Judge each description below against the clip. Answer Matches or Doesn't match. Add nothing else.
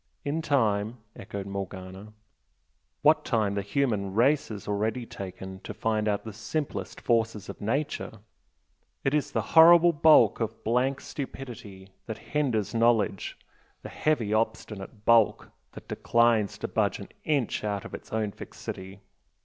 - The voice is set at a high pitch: Doesn't match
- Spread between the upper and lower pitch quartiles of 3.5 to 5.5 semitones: Matches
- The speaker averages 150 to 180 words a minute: Doesn't match